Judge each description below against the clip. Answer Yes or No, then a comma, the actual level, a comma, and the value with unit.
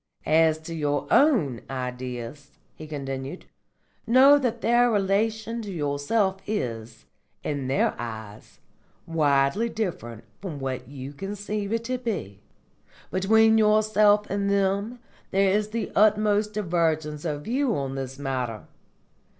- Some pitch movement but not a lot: No, wide, 7.7 semitones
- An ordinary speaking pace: No, slow, 125 wpm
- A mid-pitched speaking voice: Yes, medium, 180 Hz